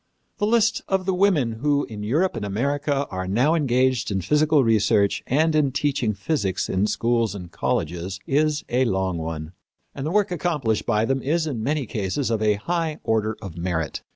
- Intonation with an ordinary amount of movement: No, wide, 6.7 semitones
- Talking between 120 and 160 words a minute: No, average, 185 wpm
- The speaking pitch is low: Yes, low, 125 Hz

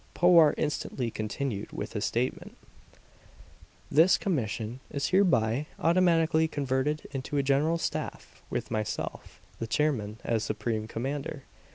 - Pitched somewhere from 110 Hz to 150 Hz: Yes, medium, 140 Hz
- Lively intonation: Yes, wide, 5.7 semitones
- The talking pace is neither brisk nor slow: No, slow, 115 wpm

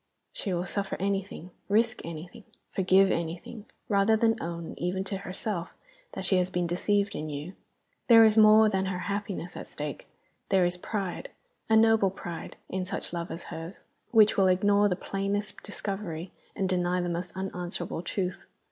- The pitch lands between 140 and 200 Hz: Yes, high, 190 Hz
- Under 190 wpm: Yes, average, 165 wpm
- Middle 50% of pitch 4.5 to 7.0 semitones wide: No, narrow, 2.5 semitones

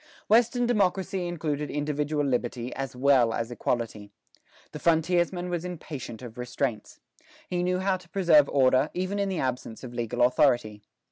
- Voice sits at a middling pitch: Yes, medium, 145 Hz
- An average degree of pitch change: No, wide, 6.4 semitones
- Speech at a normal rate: Yes, average, 150 wpm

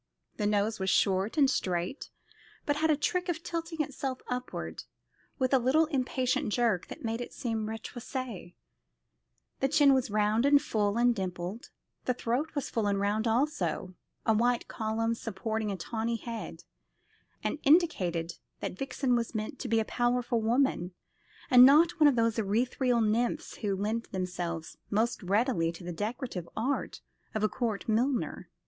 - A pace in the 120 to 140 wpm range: No, average, 160 wpm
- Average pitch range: Yes, average, 4.0 semitones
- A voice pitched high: Yes, high, 230 Hz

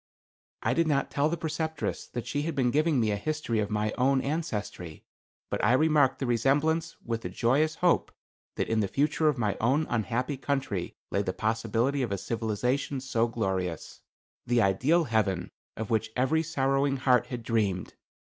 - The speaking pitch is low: Yes, low, 125 Hz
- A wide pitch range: No, average, 4.8 semitones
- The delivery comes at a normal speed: Yes, average, 175 wpm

